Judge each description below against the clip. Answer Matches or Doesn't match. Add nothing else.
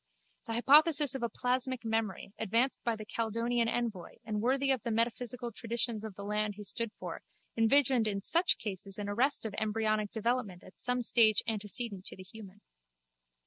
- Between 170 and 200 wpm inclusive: Matches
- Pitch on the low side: Doesn't match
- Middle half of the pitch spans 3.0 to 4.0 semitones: Doesn't match